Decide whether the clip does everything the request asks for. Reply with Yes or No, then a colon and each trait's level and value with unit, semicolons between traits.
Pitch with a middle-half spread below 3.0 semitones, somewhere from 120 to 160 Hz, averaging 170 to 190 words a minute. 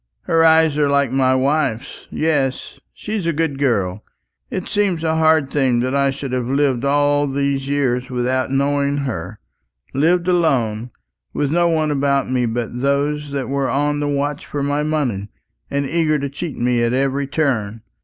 Yes: narrow, 2.5 semitones; medium, 140 Hz; average, 175 wpm